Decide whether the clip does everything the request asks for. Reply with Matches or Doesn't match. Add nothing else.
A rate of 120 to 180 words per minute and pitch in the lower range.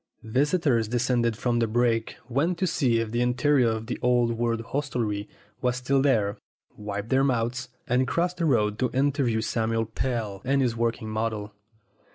Matches